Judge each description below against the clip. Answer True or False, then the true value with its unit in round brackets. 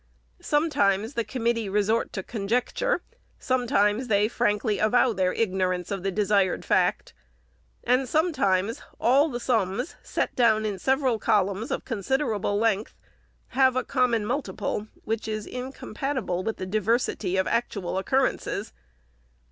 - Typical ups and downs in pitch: True (4.0 semitones)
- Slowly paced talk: True (130 wpm)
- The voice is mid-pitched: False (220 Hz)